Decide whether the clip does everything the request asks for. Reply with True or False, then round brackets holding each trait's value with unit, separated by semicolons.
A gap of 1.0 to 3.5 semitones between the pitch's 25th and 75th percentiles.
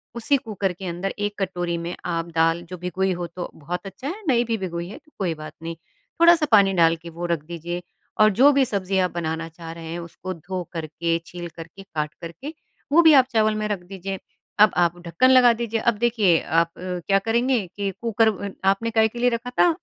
False (4.9 semitones)